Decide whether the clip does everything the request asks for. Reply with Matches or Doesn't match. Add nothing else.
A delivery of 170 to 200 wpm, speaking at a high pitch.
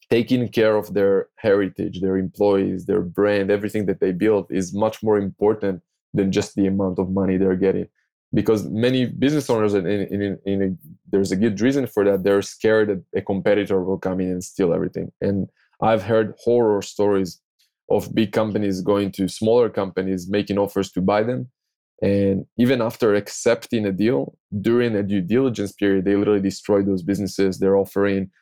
Doesn't match